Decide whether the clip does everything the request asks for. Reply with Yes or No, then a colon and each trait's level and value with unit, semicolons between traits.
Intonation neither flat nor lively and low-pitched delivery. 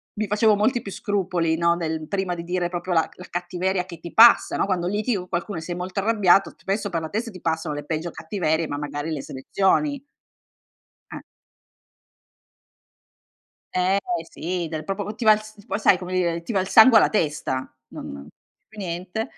No: average, 3.6 semitones; medium, 180 Hz